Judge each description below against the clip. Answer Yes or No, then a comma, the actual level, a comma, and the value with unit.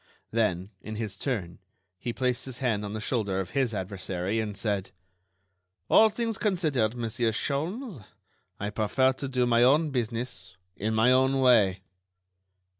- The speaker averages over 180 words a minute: No, average, 150 wpm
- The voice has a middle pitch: No, low, 115 Hz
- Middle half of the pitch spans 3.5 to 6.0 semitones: Yes, average, 4.2 semitones